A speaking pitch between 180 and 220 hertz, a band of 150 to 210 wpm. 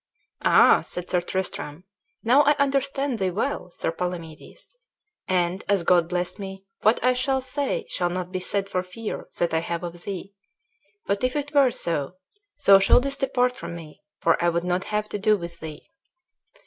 Yes: high, 190 Hz; average, 180 wpm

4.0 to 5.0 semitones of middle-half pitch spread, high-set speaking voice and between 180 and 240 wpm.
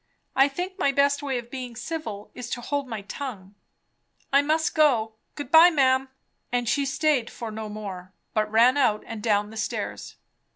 Yes: average, 4.5 semitones; very high, 250 Hz; average, 190 wpm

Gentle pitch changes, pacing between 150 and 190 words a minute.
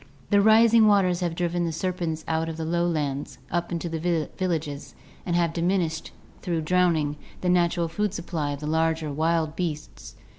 Yes: narrow, 1.9 semitones; average, 175 wpm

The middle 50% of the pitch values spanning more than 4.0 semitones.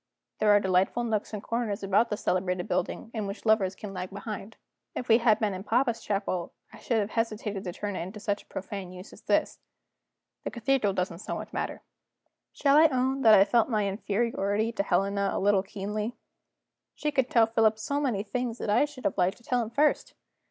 No: average, 3.0 semitones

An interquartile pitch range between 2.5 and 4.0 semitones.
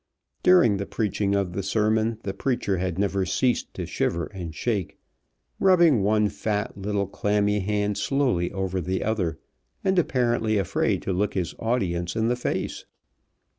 Yes: average, 2.9 semitones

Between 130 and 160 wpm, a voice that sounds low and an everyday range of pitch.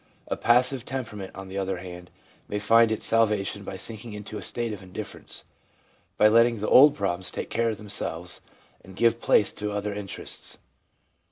No: average, 175 wpm; low, 105 Hz; average, 3.1 semitones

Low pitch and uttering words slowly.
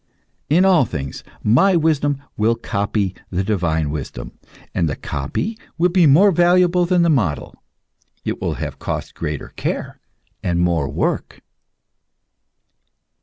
Yes: low, 115 Hz; slow, 130 wpm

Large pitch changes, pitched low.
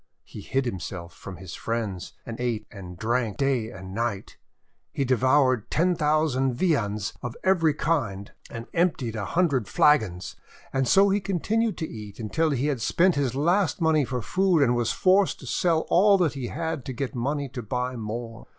Yes: wide, 6.1 semitones; low, 130 Hz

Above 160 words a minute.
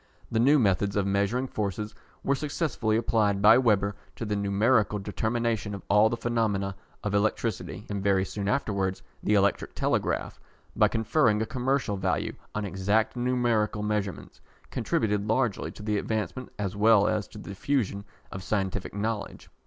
No: average, 155 wpm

